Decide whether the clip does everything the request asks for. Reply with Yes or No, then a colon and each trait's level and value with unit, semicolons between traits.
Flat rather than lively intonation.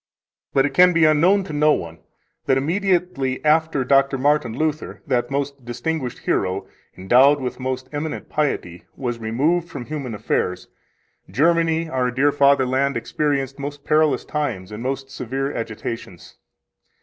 No: average, 3.3 semitones